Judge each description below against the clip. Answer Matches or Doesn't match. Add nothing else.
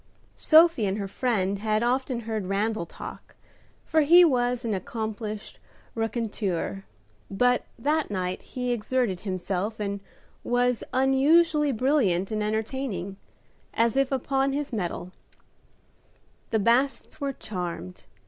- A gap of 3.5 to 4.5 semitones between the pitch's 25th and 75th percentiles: Doesn't match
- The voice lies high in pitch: Matches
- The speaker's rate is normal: Doesn't match